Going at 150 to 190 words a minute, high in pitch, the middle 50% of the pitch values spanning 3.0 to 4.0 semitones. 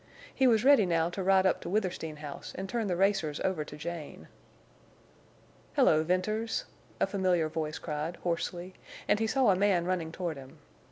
No: average, 175 wpm; medium, 180 Hz; average, 3.6 semitones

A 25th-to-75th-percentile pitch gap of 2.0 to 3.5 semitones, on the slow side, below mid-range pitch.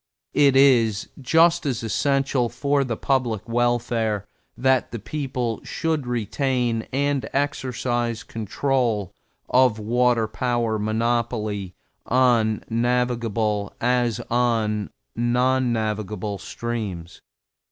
Yes: average, 2.8 semitones; slow, 95 wpm; low, 120 Hz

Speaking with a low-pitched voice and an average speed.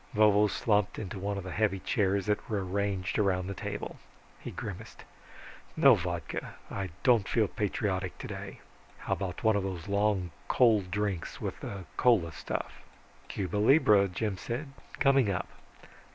Yes: low, 100 Hz; average, 150 wpm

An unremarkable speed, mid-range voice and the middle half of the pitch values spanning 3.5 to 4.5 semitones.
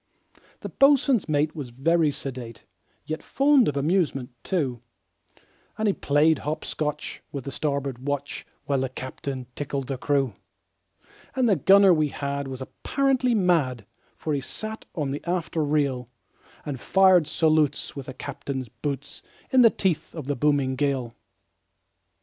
Yes: average, 150 wpm; medium, 145 Hz; average, 4.2 semitones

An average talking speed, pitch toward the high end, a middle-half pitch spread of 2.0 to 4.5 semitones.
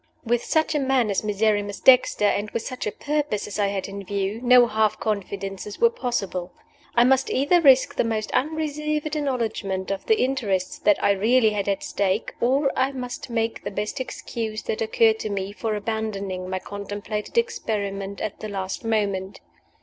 Yes: average, 180 wpm; high, 215 Hz; average, 4.2 semitones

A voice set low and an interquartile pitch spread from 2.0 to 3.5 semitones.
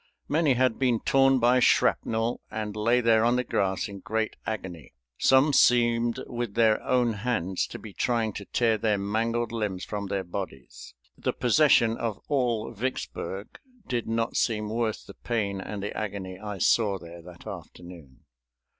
Yes: low, 110 Hz; average, 3.2 semitones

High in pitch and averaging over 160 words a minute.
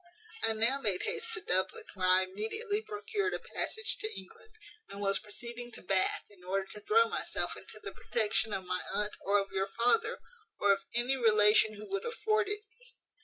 Yes: high, 225 Hz; average, 195 wpm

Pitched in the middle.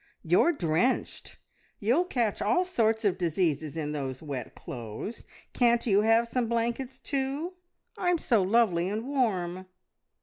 No: high, 220 Hz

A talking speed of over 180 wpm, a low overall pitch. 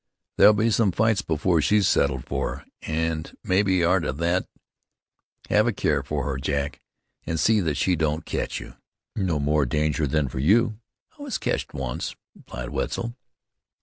No: average, 160 wpm; very low, 80 Hz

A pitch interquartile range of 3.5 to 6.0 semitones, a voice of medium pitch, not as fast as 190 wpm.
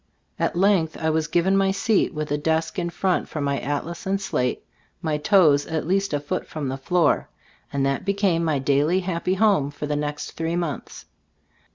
No: average, 4.2 semitones; medium, 160 Hz; average, 195 wpm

